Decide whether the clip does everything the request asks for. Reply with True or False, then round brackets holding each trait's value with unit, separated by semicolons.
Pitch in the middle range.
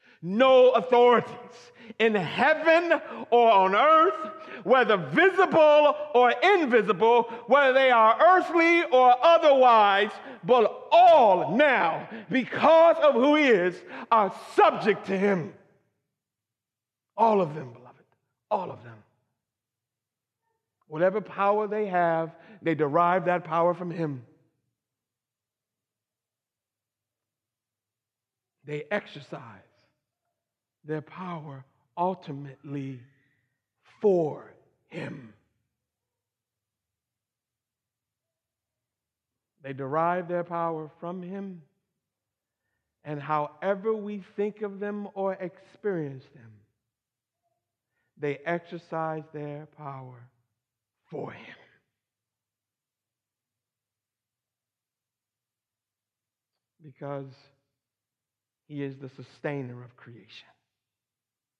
True (155 Hz)